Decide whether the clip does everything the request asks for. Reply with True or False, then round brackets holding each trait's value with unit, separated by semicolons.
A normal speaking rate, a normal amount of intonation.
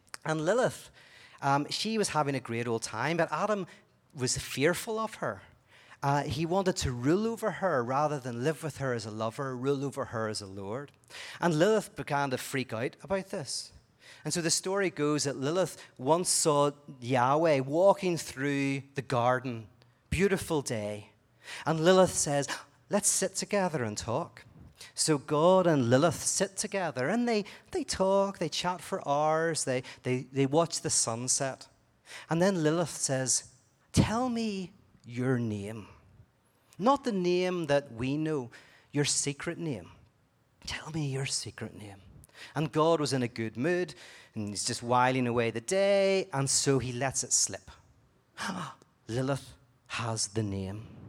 False (160 wpm; 5.8 semitones)